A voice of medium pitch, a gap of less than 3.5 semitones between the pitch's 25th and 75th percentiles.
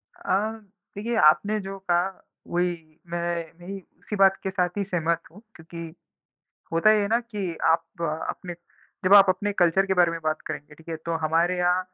Yes: medium, 180 Hz; average, 2.8 semitones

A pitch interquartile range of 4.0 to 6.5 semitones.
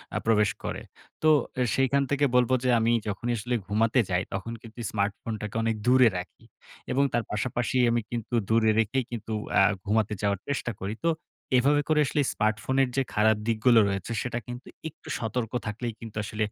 No: average, 2.8 semitones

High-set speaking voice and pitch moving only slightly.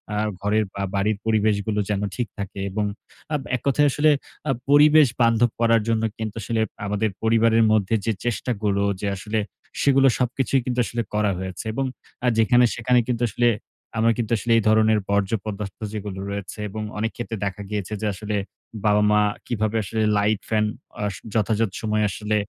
No: low, 110 Hz; narrow, 2.0 semitones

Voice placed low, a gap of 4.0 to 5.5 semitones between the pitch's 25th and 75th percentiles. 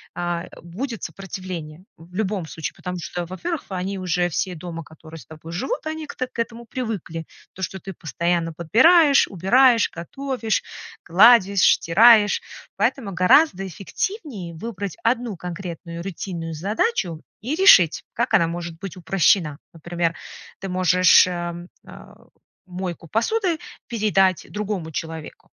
No: medium, 185 Hz; average, 5.0 semitones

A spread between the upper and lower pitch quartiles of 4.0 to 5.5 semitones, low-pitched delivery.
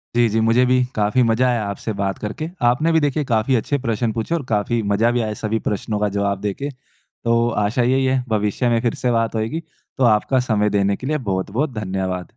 No: average, 3.4 semitones; low, 115 Hz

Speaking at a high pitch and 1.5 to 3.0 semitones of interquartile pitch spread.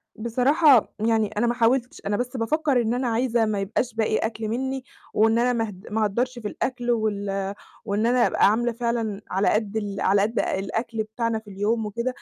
Yes: high, 225 Hz; narrow, 2.4 semitones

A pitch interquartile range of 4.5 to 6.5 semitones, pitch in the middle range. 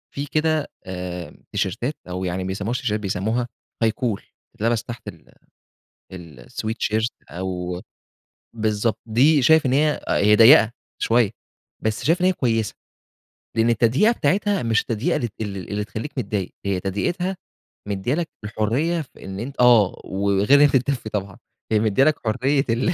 No: average, 5.3 semitones; low, 115 Hz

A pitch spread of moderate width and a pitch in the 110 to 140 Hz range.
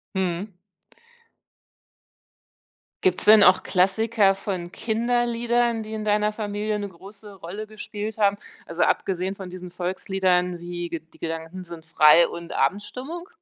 No: average, 3.3 semitones; high, 195 Hz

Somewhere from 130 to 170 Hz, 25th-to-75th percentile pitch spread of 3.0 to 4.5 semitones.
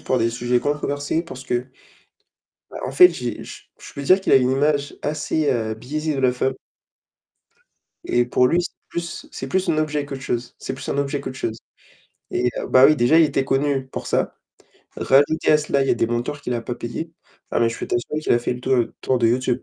Yes: low, 135 Hz; average, 3.3 semitones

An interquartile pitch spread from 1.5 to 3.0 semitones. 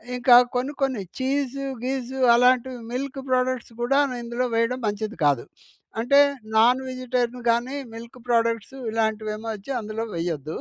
Yes: narrow, 2.4 semitones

